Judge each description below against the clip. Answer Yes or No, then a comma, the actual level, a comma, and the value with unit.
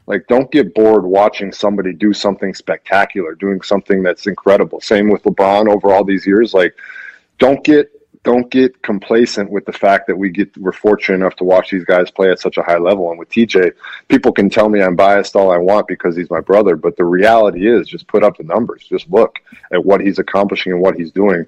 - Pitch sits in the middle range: No, low, 100 Hz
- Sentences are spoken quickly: Yes, fast, 225 wpm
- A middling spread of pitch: No, narrow, 2.1 semitones